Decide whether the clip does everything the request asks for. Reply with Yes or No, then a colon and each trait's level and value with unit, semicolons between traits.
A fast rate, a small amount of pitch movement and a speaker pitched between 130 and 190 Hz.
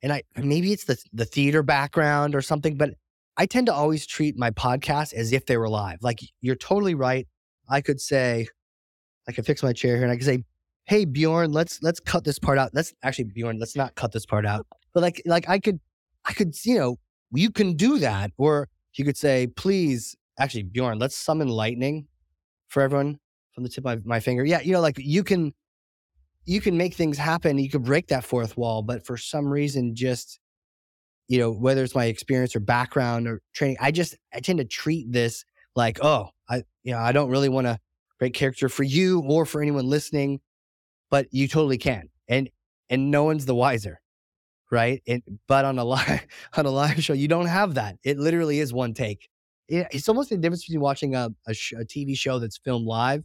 No: fast, 215 wpm; average, 4.5 semitones; low, 135 Hz